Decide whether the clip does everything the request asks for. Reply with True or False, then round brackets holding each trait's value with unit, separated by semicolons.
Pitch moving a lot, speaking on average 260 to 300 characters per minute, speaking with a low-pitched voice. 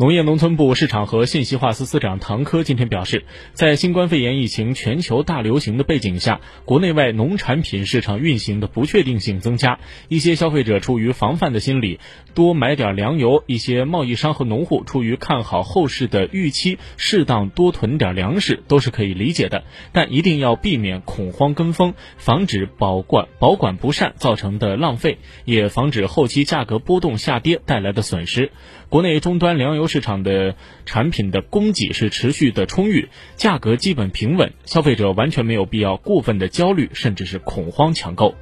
True (6.9 semitones; 290 characters per minute; 125 Hz)